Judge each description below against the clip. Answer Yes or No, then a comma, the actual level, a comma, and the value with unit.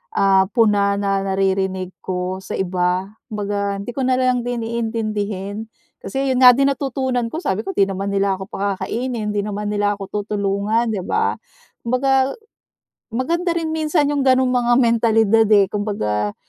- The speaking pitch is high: Yes, high, 210 Hz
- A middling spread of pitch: Yes, average, 3.9 semitones